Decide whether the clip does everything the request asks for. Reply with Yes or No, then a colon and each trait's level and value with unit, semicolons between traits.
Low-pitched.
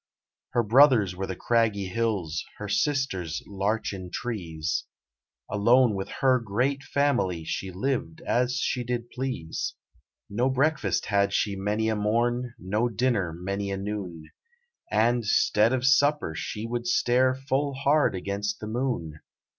Yes: low, 110 Hz